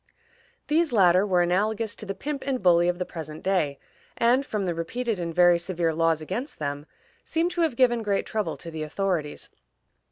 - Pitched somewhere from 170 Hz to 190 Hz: Yes, medium, 185 Hz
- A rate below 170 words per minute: No, average, 190 wpm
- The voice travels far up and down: Yes, wide, 5.7 semitones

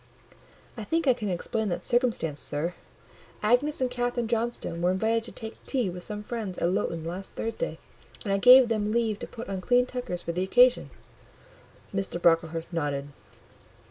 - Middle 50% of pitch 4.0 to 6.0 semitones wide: Yes, wide, 5.5 semitones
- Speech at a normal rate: Yes, average, 175 wpm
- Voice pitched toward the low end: No, high, 210 Hz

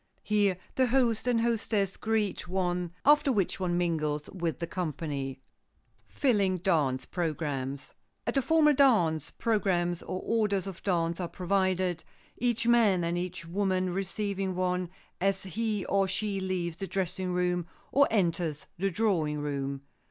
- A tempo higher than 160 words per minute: No, average, 145 wpm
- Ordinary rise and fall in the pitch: Yes, average, 3.5 semitones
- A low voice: No, medium, 185 Hz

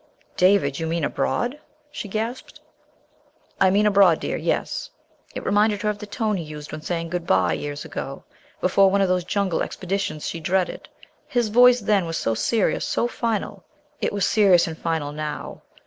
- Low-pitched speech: No, high, 190 Hz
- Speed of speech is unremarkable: Yes, average, 180 wpm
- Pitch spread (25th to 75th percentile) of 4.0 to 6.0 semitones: Yes, average, 4.4 semitones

